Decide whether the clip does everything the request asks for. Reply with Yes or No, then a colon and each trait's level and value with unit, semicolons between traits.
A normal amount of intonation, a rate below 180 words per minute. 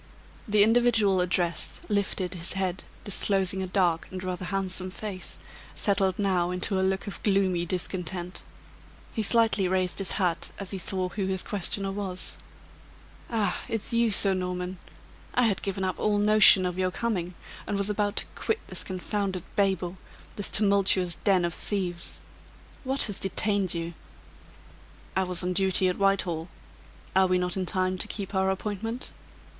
No: narrow, 1.9 semitones; average, 160 wpm